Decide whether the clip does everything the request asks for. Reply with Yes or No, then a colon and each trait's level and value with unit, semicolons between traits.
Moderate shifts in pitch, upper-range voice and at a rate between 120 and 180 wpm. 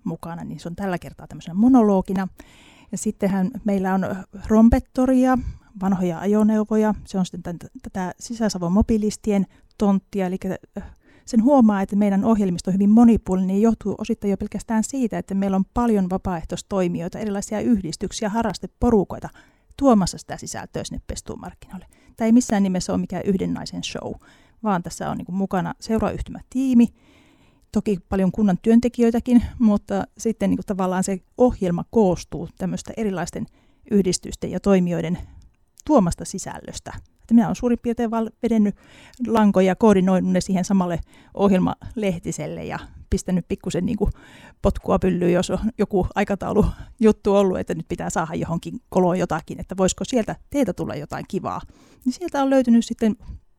Yes: average, 3.2 semitones; high, 200 Hz; average, 140 wpm